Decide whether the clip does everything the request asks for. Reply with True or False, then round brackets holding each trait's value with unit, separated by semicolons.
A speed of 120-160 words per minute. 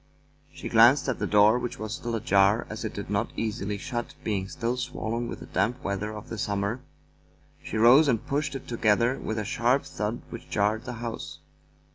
False (195 wpm)